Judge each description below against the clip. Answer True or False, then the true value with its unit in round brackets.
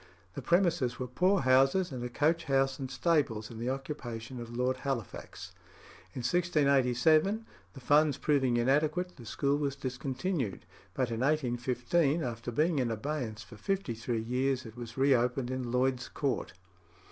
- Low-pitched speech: True (130 Hz)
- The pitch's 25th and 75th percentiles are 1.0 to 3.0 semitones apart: False (3.7 semitones)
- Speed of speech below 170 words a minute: True (160 wpm)